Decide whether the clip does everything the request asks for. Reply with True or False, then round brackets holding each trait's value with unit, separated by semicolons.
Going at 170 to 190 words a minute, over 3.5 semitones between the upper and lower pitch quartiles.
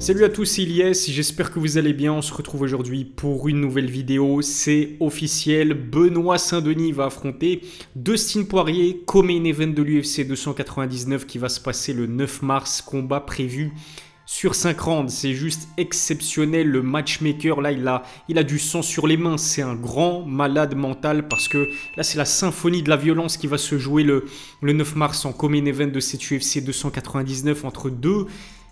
False (185 wpm; 2.9 semitones)